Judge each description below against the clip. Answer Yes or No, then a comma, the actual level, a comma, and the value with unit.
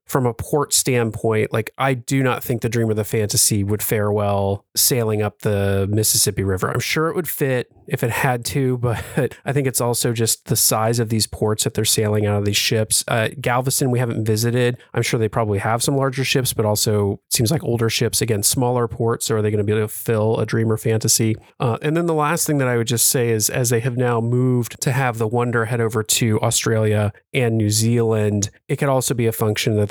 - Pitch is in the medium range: No, low, 115 Hz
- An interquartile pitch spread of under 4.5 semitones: Yes, narrow, 2.6 semitones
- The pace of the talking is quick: Yes, fast, 235 wpm